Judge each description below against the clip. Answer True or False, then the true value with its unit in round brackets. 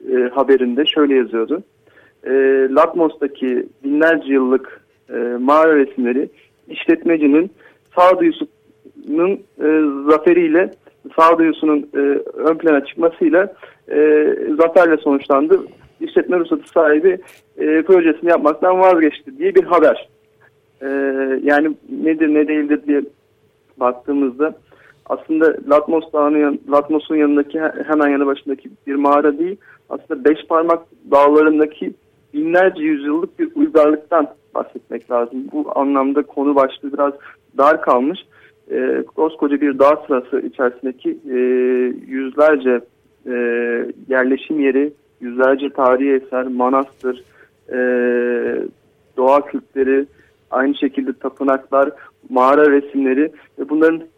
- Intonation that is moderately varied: True (3.2 semitones)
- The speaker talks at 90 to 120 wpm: True (105 wpm)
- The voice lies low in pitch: False (145 Hz)